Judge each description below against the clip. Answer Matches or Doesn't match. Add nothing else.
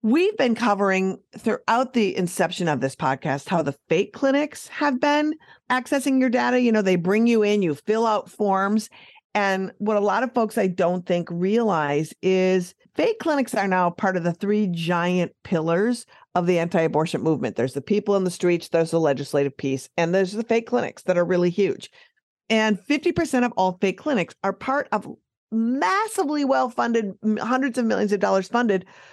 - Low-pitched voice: Doesn't match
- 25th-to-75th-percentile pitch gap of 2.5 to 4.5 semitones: Doesn't match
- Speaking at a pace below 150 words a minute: Doesn't match